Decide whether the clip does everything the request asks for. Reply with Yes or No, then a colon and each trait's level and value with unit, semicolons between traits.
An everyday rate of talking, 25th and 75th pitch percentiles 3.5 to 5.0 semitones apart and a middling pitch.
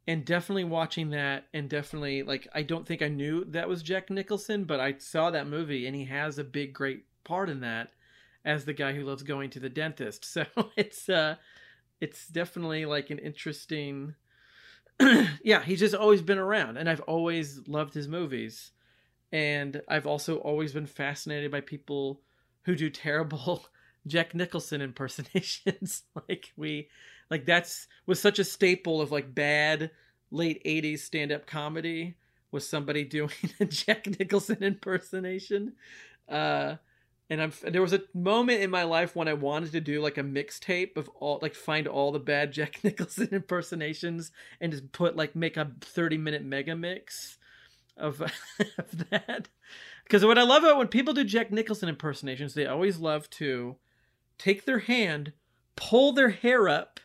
Yes: average, 170 wpm; average, 4.2 semitones; medium, 155 Hz